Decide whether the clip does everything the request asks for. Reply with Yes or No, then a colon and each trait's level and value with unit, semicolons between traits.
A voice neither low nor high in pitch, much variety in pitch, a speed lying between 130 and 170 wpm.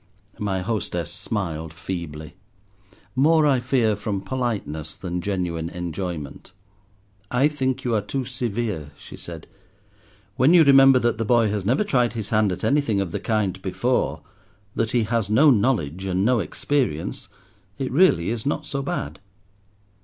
No: low, 110 Hz; wide, 6.1 semitones; average, 155 wpm